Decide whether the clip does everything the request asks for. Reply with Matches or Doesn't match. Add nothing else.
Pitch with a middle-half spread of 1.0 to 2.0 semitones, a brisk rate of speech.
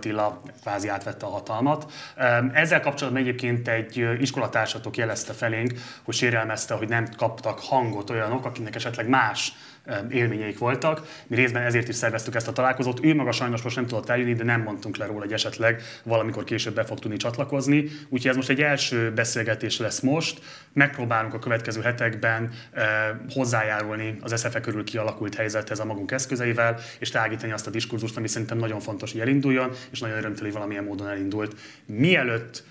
Doesn't match